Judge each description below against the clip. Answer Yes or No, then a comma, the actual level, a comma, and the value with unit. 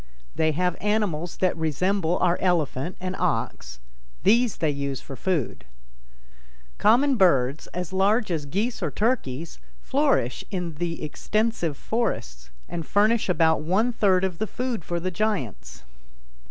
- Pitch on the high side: No, medium, 180 Hz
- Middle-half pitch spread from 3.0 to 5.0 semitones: No, wide, 5.5 semitones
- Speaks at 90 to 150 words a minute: Yes, average, 140 wpm